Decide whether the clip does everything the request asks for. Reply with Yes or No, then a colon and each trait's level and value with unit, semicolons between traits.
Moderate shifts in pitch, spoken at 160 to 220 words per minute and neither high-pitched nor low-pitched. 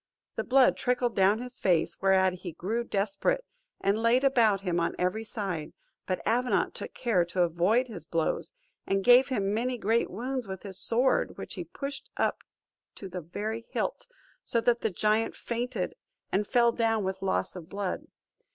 No: average, 4.2 semitones; average, 175 wpm; high, 215 Hz